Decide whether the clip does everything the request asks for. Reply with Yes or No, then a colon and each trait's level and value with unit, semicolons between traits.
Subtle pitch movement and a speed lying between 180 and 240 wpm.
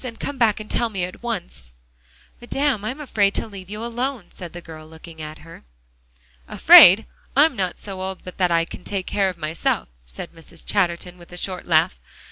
No: average, 4.7 semitones; average, 200 wpm